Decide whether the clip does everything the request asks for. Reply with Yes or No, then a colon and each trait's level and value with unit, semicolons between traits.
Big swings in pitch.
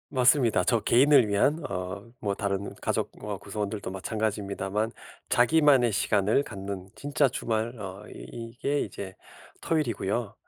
No: average, 4.0 semitones